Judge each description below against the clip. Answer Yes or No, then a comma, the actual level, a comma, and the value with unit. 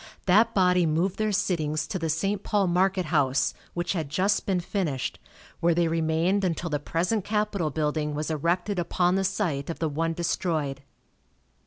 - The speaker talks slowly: No, average, 170 wpm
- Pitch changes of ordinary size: Yes, average, 3.4 semitones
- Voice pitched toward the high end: No, medium, 170 Hz